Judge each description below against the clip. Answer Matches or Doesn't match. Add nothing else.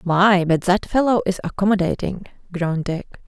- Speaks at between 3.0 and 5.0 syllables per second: Doesn't match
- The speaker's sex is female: Matches